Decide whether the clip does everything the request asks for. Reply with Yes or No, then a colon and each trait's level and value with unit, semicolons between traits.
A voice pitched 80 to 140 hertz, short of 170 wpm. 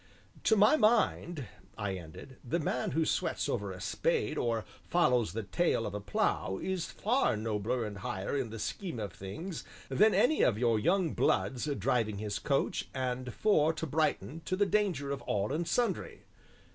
No: low, 135 Hz; average, 175 wpm